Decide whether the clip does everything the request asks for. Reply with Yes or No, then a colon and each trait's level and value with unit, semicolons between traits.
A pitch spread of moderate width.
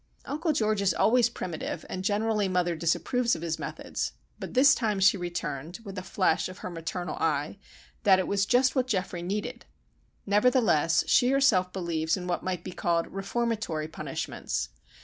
Yes: average, 4.7 semitones